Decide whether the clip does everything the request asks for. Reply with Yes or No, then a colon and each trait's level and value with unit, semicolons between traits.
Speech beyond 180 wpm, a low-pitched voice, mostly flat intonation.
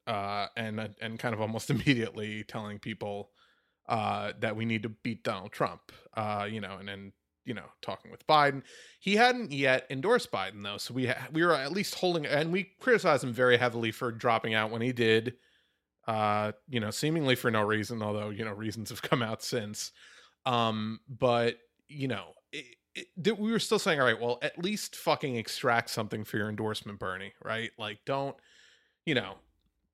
No: average, 190 wpm; low, 115 Hz; average, 4.3 semitones